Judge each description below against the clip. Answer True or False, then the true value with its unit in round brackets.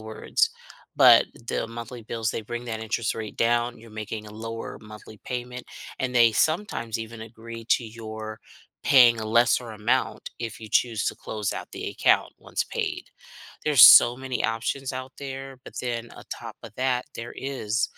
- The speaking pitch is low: True (115 Hz)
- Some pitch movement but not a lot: False (2.1 semitones)